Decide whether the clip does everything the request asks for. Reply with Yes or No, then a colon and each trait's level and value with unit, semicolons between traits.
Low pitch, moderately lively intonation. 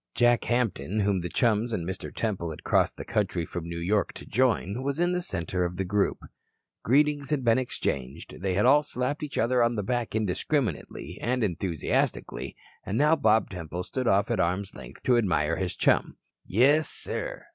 No: low, 110 Hz; wide, 5.8 semitones